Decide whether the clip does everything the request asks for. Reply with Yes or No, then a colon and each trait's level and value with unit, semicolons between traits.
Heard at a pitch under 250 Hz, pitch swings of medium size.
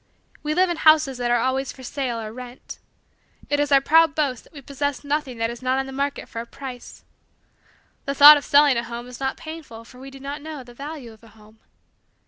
No: very high, 270 Hz; average, 3.2 semitones